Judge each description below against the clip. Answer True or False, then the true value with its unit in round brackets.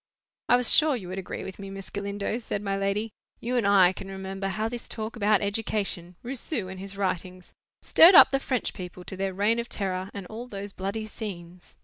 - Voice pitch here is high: True (200 Hz)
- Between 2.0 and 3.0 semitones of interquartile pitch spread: True (2.7 semitones)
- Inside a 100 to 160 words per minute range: False (205 wpm)